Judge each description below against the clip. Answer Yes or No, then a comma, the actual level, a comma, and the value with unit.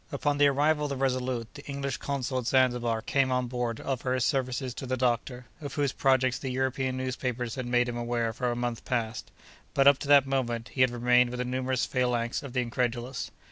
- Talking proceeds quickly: Yes, fast, 220 wpm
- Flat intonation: Yes, narrow, 1.7 semitones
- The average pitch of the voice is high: No, low, 130 Hz